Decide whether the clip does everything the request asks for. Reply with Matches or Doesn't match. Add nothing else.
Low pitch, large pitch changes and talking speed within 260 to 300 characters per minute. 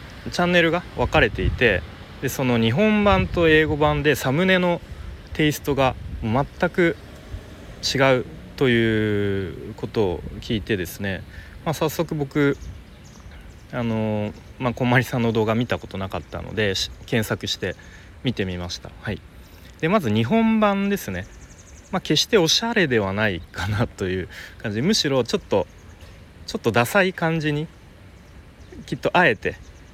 Matches